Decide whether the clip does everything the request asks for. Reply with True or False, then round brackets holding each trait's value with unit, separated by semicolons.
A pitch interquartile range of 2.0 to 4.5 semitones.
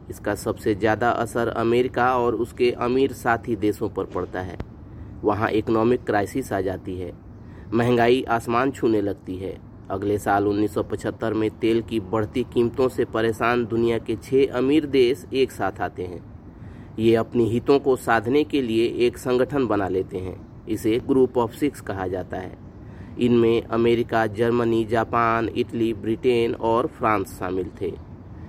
True (2.6 semitones)